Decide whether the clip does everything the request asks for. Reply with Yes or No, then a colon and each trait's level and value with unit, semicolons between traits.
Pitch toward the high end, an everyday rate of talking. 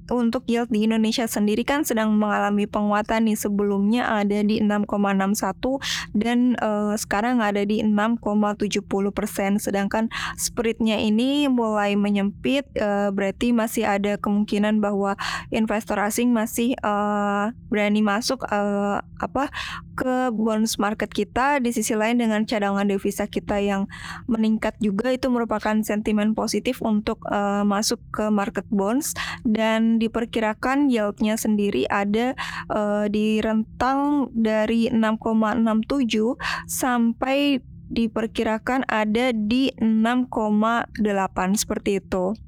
Yes: high, 215 Hz; average, 115 wpm